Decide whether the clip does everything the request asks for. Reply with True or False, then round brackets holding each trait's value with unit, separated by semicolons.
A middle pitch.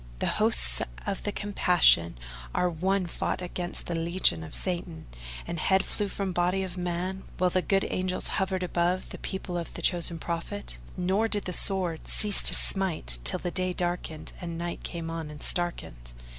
True (180 Hz)